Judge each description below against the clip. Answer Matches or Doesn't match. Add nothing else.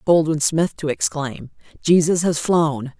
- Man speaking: Doesn't match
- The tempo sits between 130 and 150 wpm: Matches